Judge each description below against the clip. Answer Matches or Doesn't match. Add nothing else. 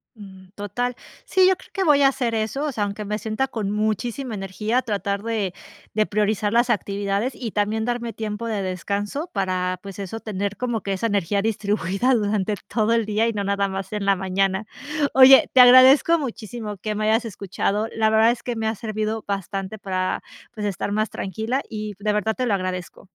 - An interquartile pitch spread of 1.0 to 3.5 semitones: Matches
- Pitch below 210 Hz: Doesn't match